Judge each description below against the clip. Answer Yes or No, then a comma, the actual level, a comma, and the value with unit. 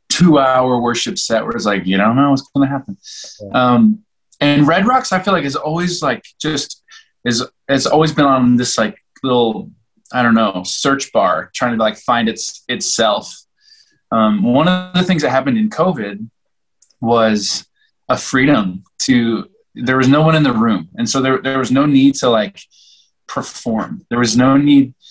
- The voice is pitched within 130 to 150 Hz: Yes, low, 135 Hz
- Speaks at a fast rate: No, average, 185 wpm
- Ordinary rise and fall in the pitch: No, wide, 6.6 semitones